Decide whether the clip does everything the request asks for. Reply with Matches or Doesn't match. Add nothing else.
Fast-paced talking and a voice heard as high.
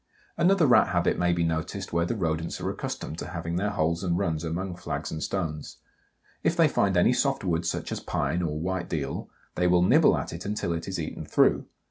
Doesn't match